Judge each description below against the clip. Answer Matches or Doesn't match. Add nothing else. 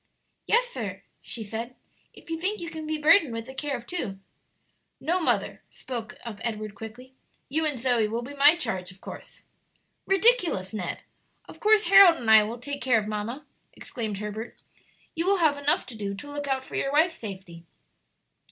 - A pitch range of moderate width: Doesn't match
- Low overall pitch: Doesn't match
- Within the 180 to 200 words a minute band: Matches